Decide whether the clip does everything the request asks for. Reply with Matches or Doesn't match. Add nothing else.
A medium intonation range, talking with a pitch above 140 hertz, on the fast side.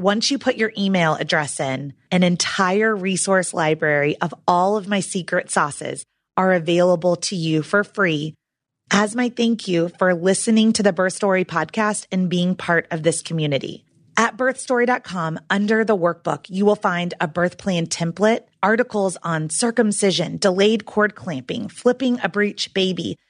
Doesn't match